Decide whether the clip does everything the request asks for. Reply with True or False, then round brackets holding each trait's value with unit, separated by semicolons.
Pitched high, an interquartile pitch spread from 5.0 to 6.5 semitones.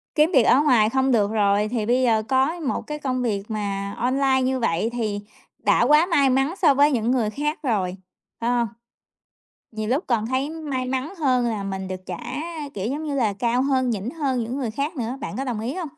False (250 Hz; 4.2 semitones)